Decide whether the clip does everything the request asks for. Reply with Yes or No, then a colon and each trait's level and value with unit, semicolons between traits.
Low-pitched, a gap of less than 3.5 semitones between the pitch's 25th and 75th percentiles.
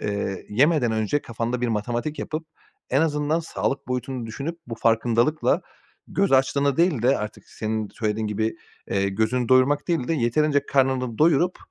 No: low, 125 Hz; average, 4.7 semitones